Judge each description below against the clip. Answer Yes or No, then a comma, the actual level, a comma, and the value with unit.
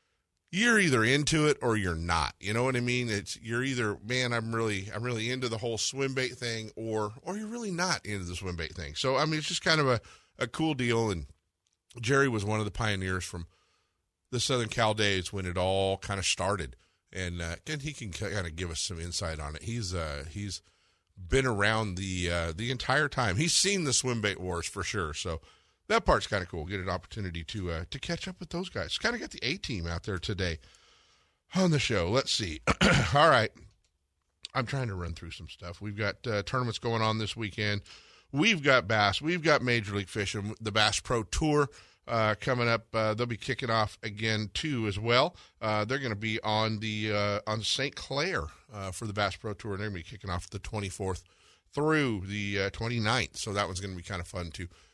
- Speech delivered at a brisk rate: Yes, fast, 225 wpm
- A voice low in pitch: Yes, low, 105 Hz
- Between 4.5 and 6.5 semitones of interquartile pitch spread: Yes, average, 4.8 semitones